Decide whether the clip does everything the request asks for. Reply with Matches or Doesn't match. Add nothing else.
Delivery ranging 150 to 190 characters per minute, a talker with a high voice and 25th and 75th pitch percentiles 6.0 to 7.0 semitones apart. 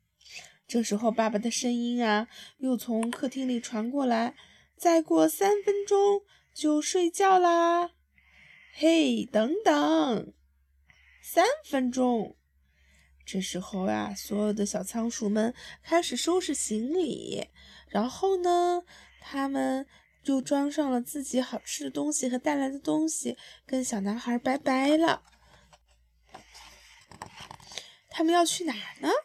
Matches